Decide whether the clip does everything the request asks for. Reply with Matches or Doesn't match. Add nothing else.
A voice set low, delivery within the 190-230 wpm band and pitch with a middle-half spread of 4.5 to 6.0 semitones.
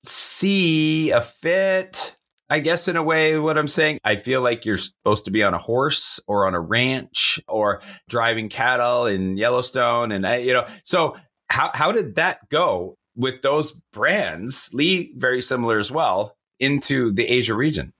Doesn't match